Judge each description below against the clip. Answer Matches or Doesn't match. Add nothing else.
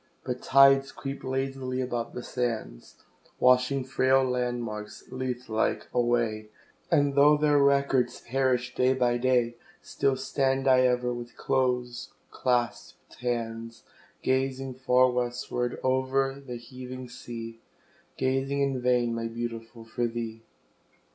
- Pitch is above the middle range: Doesn't match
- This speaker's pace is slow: Matches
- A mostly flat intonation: Matches